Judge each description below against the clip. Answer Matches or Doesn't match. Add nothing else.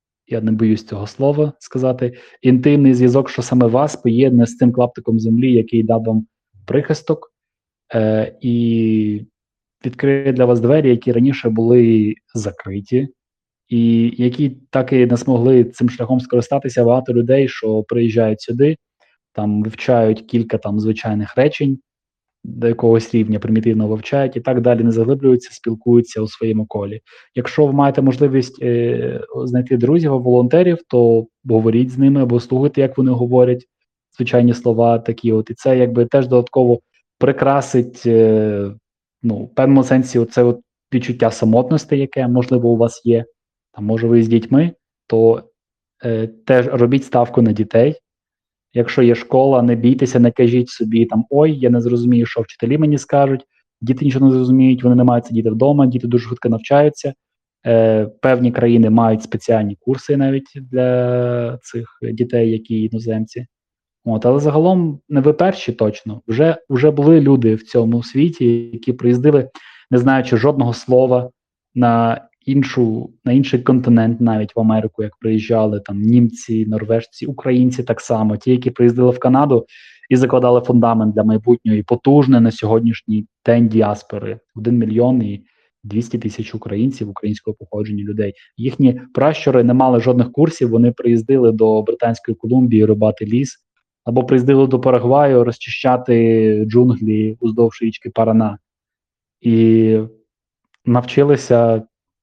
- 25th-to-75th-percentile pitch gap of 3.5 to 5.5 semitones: Doesn't match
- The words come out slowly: Doesn't match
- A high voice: Doesn't match